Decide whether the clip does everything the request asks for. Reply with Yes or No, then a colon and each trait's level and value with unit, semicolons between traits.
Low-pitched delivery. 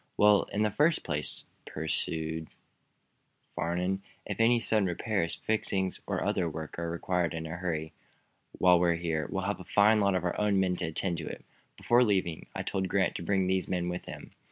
Yes: very low, 90 Hz